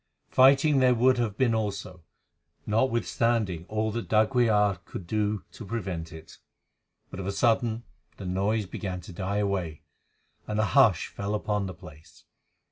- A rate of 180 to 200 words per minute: No, average, 150 wpm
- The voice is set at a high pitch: No, low, 105 Hz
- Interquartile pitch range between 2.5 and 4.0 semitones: Yes, average, 3.5 semitones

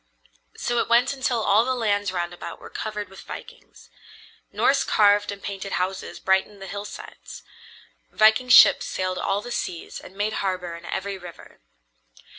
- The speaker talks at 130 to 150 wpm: No, average, 160 wpm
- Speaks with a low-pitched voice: No, high, 200 Hz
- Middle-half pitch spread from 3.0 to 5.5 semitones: No, narrow, 2.5 semitones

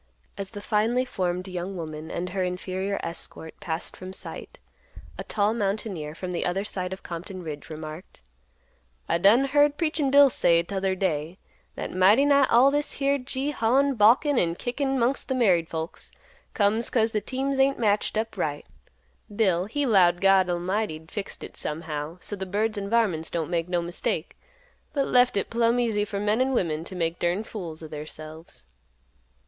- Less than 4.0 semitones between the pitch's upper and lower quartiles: No, wide, 5.4 semitones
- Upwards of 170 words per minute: Yes, average, 180 wpm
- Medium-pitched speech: No, high, 195 Hz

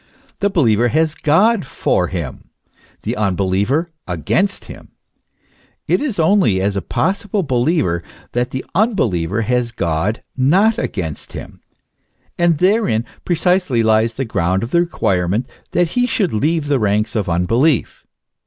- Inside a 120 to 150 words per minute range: Yes, average, 140 wpm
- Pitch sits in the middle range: No, low, 125 Hz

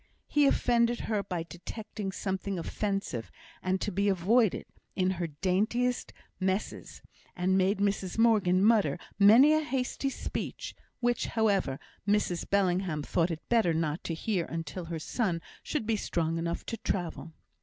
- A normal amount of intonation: Yes, average, 4.3 semitones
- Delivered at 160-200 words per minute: No, average, 145 wpm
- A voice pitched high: Yes, high, 195 Hz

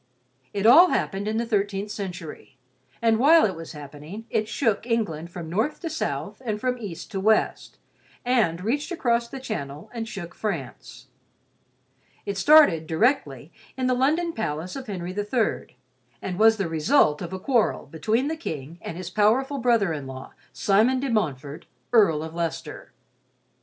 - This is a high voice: Yes, high, 210 Hz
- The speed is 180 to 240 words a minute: No, average, 165 wpm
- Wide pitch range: Yes, wide, 6.5 semitones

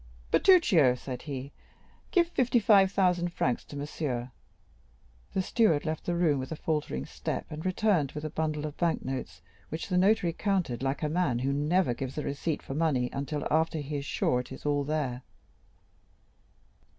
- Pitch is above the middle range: No, medium, 150 Hz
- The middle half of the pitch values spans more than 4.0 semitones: Yes, average, 4.5 semitones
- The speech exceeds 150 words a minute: Yes, average, 175 wpm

